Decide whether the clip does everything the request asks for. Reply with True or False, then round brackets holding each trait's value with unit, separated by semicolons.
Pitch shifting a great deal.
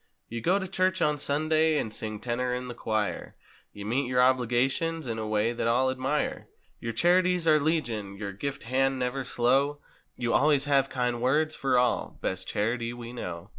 False (4.1 semitones)